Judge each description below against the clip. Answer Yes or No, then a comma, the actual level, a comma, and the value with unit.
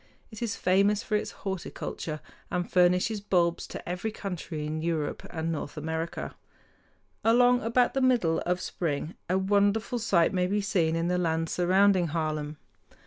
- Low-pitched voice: No, medium, 180 Hz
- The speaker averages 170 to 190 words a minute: No, average, 155 wpm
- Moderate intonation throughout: Yes, average, 3.9 semitones